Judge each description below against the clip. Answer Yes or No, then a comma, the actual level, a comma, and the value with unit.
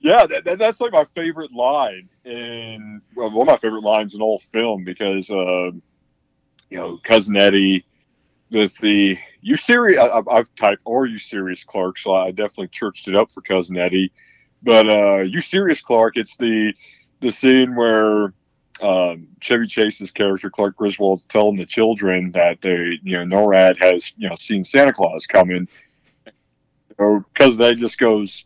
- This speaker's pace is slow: No, average, 175 wpm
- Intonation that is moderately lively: Yes, average, 3.6 semitones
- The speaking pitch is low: Yes, low, 105 Hz